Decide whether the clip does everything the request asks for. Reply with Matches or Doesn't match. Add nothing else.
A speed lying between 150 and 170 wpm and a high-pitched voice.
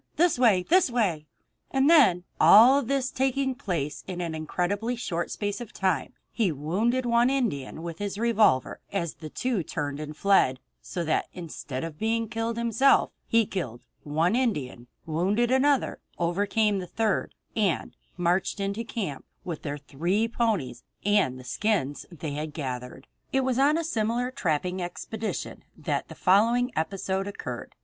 Matches